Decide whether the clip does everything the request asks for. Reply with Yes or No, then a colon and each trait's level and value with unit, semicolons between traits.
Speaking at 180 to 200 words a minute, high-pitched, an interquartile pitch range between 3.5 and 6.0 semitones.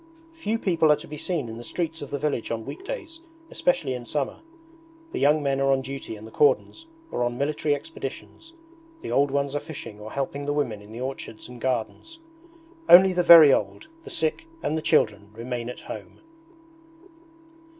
No: average, 190 wpm; medium, 140 Hz; average, 4.9 semitones